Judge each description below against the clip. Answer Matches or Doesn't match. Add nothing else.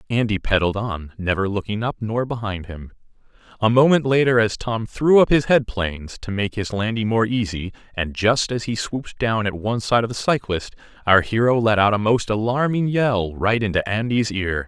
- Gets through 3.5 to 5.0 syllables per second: Doesn't match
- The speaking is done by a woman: Doesn't match